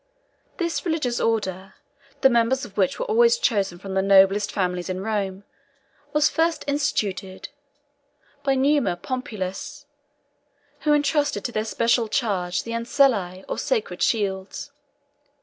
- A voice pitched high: Yes, high, 225 Hz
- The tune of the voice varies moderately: No, wide, 6.7 semitones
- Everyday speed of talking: No, slow, 130 wpm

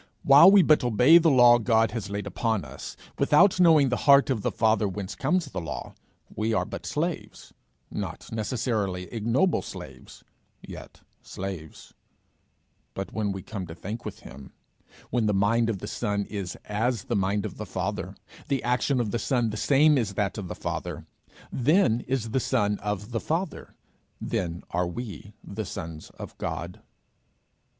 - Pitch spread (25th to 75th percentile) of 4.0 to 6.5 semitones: Yes, average, 4.3 semitones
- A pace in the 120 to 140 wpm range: No, average, 170 wpm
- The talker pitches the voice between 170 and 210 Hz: No, low, 110 Hz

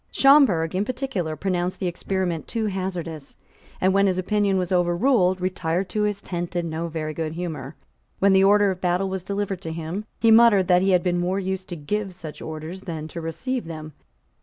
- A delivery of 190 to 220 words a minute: Yes, average, 200 wpm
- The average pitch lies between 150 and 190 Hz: Yes, medium, 185 Hz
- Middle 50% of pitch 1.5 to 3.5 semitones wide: Yes, average, 2.9 semitones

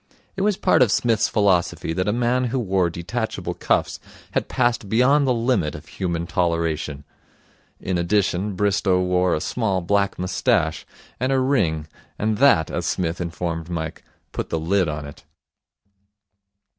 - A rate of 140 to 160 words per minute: Yes, average, 155 wpm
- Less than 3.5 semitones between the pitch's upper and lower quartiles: No, wide, 5.6 semitones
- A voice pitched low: Yes, very low, 95 Hz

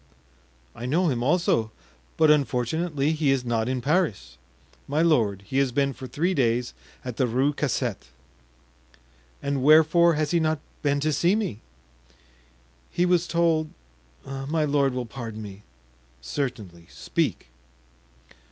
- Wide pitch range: No, average, 5.0 semitones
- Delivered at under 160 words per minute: Yes, slow, 135 wpm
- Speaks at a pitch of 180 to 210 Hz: No, low, 135 Hz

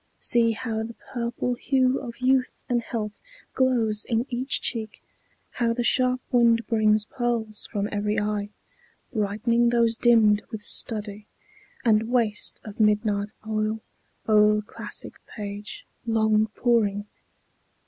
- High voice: Yes, high, 225 Hz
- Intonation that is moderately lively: No, narrow, 2.1 semitones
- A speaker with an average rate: No, slow, 125 wpm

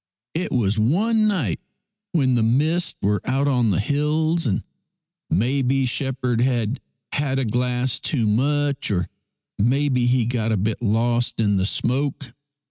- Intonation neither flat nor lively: Yes, average, 4.1 semitones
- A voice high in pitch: No, low, 125 Hz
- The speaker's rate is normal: Yes, average, 150 wpm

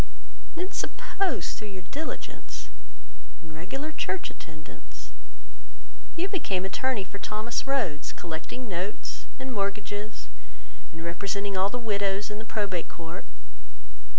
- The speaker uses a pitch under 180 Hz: No, high, 205 Hz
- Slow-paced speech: Yes, slow, 125 wpm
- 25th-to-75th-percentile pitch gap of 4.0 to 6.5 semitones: Yes, average, 5.3 semitones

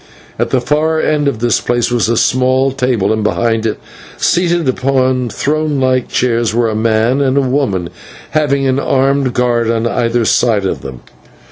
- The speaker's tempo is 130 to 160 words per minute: No, average, 175 wpm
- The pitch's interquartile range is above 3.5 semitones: No, average, 3.0 semitones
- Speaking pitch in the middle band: No, low, 125 Hz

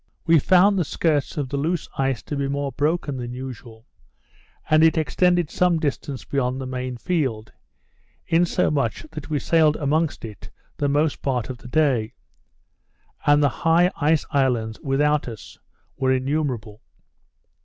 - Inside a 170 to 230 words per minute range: No, average, 150 wpm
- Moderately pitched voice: Yes, medium, 145 Hz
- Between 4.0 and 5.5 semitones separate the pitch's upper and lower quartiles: No, average, 3.5 semitones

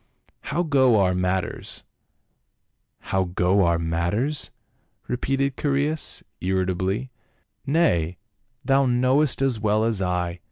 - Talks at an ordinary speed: No, slow, 130 wpm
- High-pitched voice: No, low, 105 Hz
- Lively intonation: Yes, wide, 7.0 semitones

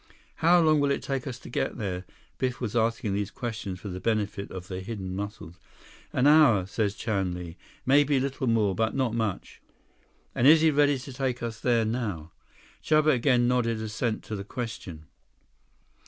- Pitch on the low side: Yes, low, 115 Hz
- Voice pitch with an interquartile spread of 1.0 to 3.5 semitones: No, average, 4.5 semitones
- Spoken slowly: No, average, 180 wpm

